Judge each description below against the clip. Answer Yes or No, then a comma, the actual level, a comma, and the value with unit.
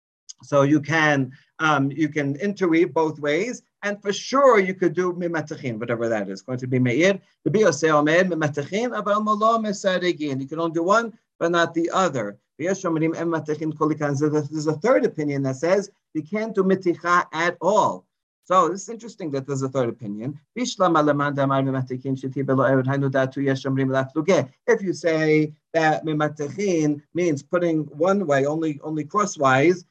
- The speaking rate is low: Yes, slow, 125 wpm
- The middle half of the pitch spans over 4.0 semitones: Yes, average, 4.4 semitones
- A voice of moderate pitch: Yes, medium, 155 Hz